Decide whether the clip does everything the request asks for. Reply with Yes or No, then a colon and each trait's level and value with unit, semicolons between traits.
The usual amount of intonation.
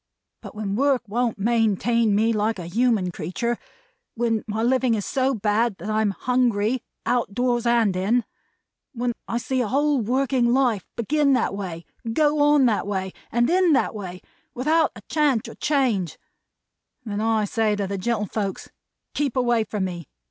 Yes: average, 3.6 semitones